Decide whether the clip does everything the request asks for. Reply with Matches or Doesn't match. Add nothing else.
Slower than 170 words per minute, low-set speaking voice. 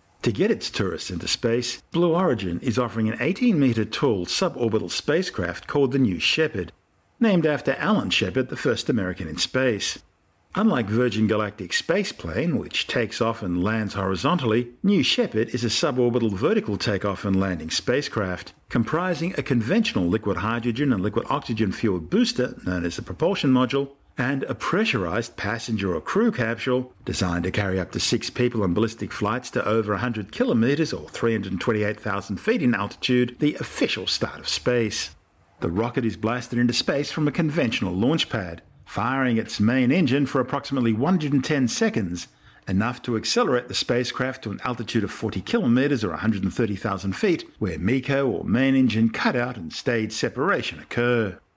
Matches